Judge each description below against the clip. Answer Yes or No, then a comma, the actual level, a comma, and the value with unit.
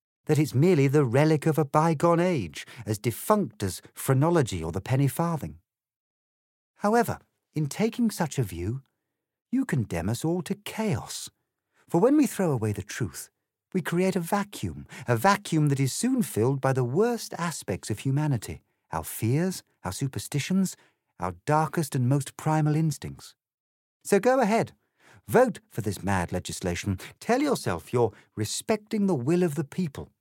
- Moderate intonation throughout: No, wide, 8.5 semitones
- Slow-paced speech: No, average, 155 wpm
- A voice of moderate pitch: Yes, medium, 150 Hz